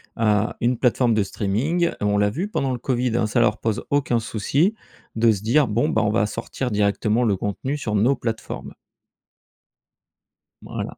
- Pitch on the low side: Yes, low, 115 Hz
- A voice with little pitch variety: No, average, 3.3 semitones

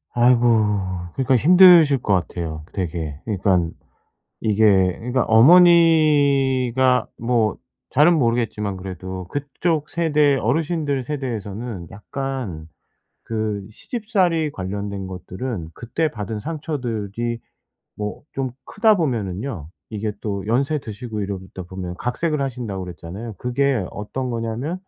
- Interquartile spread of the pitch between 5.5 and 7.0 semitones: Yes, wide, 6.1 semitones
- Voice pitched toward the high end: No, low, 120 Hz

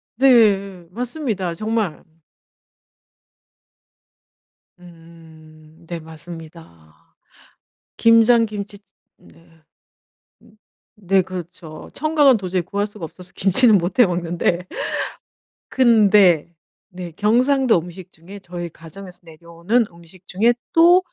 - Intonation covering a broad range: No, average, 4.5 semitones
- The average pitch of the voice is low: No, medium, 185 Hz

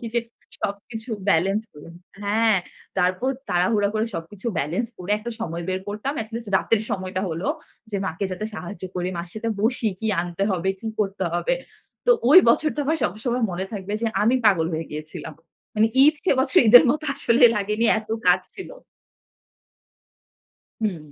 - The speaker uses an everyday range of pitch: Yes, average, 4.1 semitones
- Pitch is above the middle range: Yes, high, 205 Hz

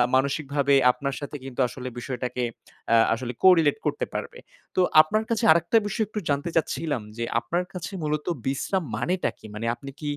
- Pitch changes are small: No, average, 5.3 semitones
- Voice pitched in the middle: Yes, medium, 145 Hz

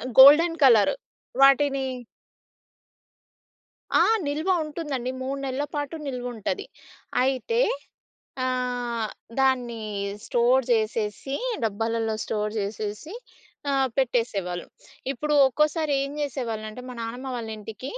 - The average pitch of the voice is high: Yes, very high, 250 Hz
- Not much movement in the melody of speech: No, average, 3.5 semitones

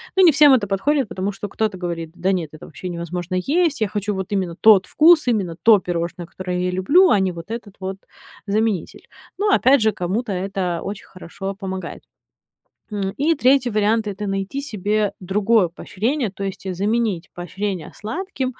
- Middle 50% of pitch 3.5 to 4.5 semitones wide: Yes, average, 3.9 semitones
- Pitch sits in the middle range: No, high, 200 Hz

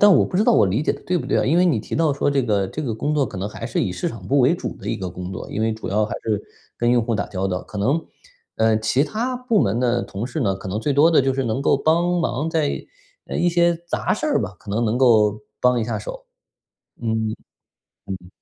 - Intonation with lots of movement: Yes, wide, 6.7 semitones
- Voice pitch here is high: No, low, 120 Hz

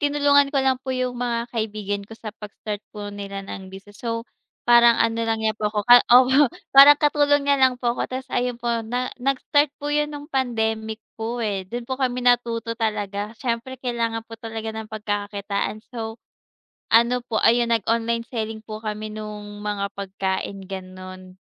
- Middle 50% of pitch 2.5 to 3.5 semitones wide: Yes, average, 3.0 semitones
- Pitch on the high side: Yes, high, 230 Hz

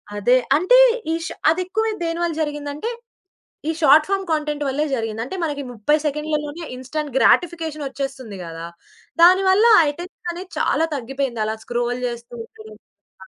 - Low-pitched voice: No, very high, 295 Hz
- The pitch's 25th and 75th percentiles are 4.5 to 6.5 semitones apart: Yes, average, 4.9 semitones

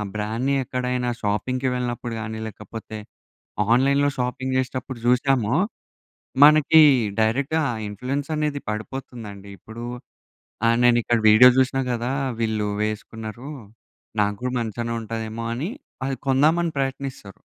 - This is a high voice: No, low, 125 Hz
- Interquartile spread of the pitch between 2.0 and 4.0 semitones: Yes, average, 3.3 semitones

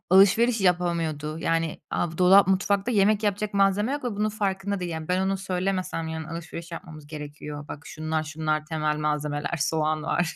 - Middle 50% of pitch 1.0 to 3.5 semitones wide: No, average, 3.9 semitones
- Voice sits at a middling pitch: Yes, medium, 170 Hz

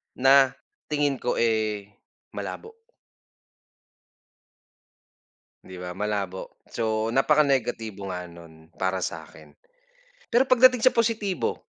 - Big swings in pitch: Yes, wide, 7.9 semitones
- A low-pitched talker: Yes, low, 115 Hz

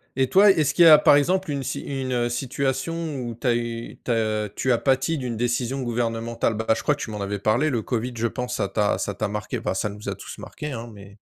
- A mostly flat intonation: No, average, 3.5 semitones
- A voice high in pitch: No, low, 120 Hz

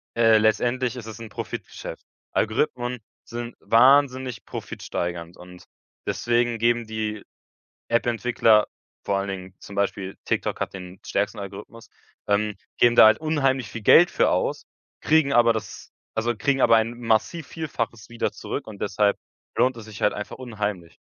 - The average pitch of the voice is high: No, low, 115 Hz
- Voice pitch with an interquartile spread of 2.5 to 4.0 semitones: Yes, average, 2.8 semitones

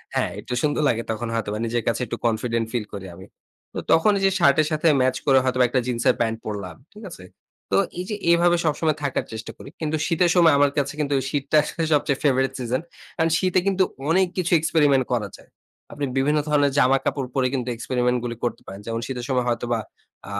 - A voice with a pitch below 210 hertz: Yes, low, 135 Hz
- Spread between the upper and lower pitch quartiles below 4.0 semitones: No, average, 4.5 semitones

